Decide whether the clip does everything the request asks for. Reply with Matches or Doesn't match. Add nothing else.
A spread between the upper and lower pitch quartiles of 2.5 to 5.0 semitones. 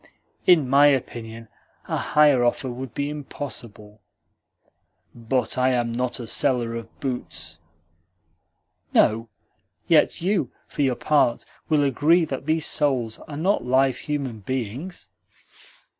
Matches